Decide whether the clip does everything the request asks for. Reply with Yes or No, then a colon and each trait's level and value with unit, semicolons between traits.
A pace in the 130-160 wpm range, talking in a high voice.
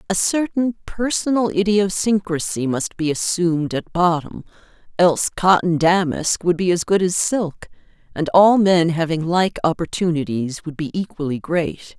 No: average, 140 wpm; medium, 175 Hz